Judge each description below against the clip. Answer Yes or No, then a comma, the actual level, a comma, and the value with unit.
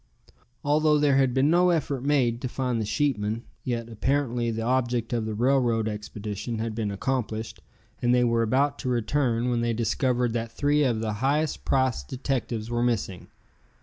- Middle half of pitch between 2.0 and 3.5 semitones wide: Yes, average, 3.1 semitones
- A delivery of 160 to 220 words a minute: Yes, average, 175 wpm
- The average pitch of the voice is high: No, low, 120 Hz